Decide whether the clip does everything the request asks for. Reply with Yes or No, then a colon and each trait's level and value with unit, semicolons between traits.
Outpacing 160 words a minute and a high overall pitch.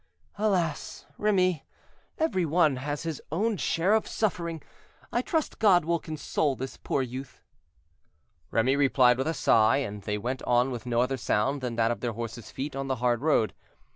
No: average, 175 wpm; low, 135 Hz